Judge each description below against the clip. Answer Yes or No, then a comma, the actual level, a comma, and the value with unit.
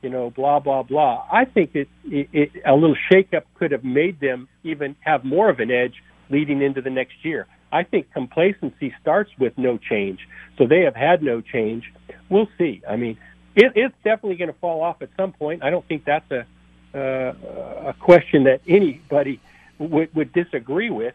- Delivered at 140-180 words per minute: No, average, 200 wpm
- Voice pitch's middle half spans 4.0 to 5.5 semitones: Yes, average, 4.5 semitones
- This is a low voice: No, medium, 145 Hz